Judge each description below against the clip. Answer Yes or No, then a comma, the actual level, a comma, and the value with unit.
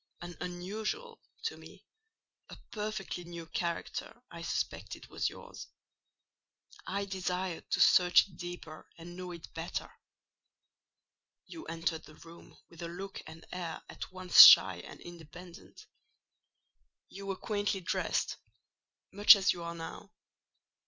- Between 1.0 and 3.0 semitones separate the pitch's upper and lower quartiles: Yes, average, 2.7 semitones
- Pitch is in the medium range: Yes, medium, 175 Hz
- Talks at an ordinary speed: No, slow, 120 wpm